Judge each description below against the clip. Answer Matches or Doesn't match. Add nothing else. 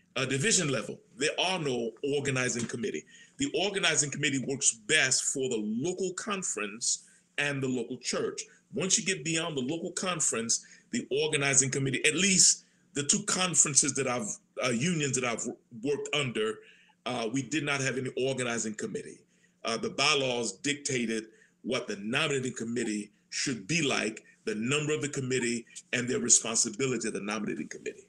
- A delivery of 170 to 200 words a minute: Doesn't match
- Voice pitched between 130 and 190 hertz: Matches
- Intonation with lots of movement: Matches